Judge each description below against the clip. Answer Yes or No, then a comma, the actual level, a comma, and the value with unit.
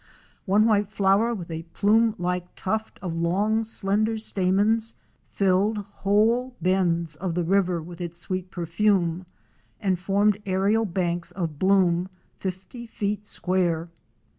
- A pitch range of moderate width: Yes, average, 3.1 semitones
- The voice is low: No, high, 190 Hz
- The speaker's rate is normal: No, slow, 130 wpm